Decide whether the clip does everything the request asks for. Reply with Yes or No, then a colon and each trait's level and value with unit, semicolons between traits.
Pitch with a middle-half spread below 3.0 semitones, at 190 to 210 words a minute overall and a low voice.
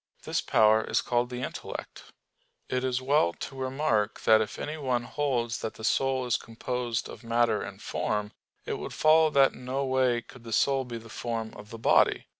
Yes: narrow, 2.6 semitones; average, 195 wpm; low, 125 Hz